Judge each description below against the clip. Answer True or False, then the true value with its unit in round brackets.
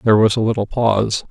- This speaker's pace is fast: True (230 wpm)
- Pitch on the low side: True (110 Hz)